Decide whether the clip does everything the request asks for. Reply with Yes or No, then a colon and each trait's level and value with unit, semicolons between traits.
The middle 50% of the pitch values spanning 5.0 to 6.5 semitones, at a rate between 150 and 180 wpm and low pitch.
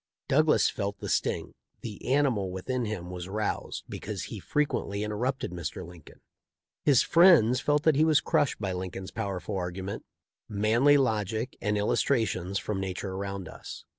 Yes: wide, 5.4 semitones; average, 160 wpm; low, 105 Hz